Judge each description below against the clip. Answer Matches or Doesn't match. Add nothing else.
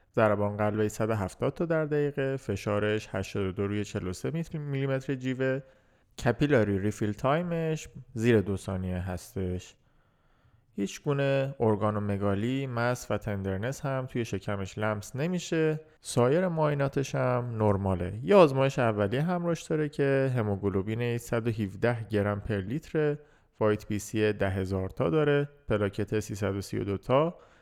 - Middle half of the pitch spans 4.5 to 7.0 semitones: Matches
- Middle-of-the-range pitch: Doesn't match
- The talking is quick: Doesn't match